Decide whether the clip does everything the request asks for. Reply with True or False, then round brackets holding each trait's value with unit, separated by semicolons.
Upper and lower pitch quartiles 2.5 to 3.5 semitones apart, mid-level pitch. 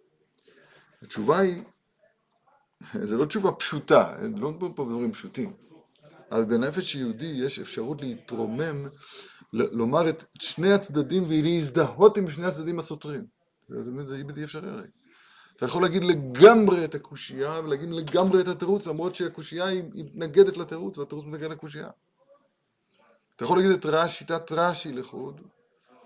False (4.2 semitones; 165 Hz)